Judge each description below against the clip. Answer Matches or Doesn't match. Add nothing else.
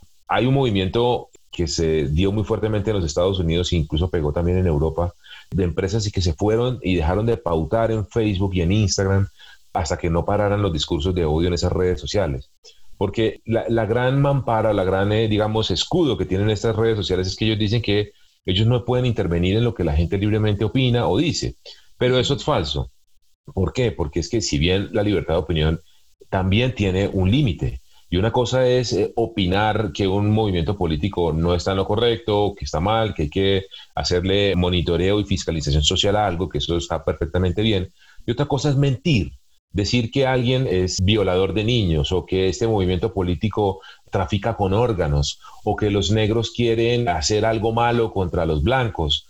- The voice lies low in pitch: Matches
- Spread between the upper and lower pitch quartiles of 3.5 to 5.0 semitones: Matches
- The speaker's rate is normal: Doesn't match